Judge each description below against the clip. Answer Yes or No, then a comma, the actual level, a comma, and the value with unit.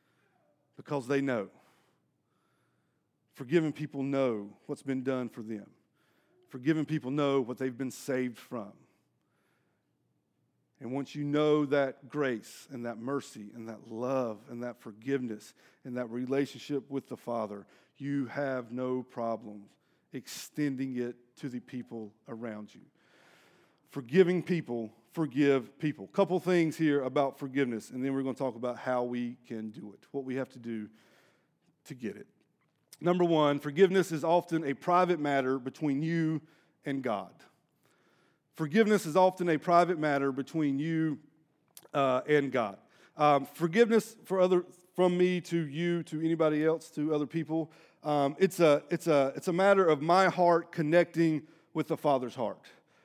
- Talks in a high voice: No, medium, 140 Hz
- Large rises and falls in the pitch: No, average, 4.1 semitones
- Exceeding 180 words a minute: No, average, 150 wpm